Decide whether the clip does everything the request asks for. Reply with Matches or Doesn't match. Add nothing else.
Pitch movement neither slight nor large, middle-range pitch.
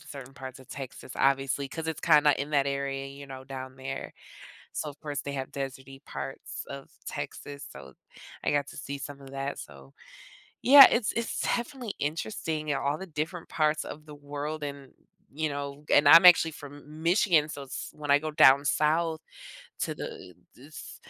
Doesn't match